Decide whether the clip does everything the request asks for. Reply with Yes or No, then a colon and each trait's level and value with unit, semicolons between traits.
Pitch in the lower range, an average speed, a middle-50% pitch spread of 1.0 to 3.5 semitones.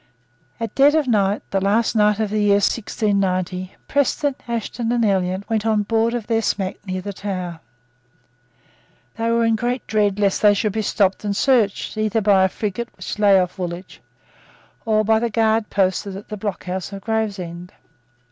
No: high, 210 Hz; average, 175 wpm; narrow, 2.6 semitones